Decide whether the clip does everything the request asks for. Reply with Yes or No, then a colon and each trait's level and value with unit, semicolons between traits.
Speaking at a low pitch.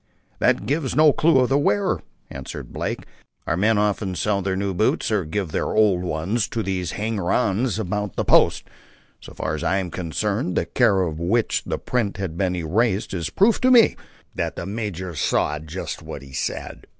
Yes: low, 100 Hz